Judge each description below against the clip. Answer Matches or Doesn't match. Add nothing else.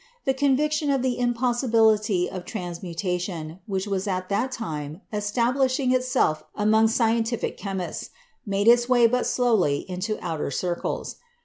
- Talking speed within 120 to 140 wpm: Matches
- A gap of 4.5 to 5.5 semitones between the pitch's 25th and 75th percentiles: Matches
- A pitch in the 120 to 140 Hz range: Doesn't match